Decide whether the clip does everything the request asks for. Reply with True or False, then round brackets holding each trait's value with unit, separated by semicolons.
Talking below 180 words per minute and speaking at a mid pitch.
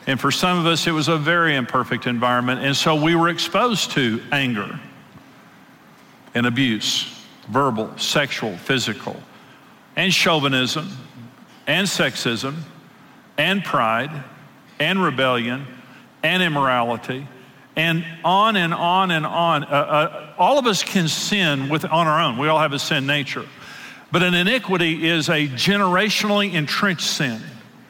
True (140 wpm; 155 Hz)